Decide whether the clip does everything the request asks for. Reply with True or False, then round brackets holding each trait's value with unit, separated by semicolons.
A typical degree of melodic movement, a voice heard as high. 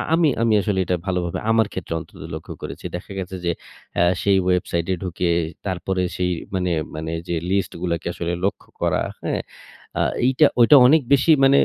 False (4.2 semitones; 95 Hz)